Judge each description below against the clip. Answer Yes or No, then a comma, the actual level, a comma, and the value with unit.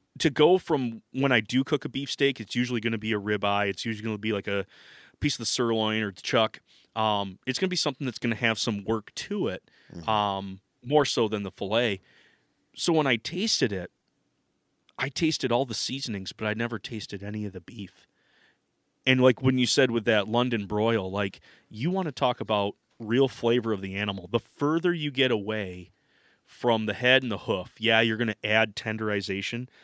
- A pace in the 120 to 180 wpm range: No, average, 200 wpm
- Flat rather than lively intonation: No, average, 3.8 semitones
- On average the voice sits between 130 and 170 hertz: No, low, 115 Hz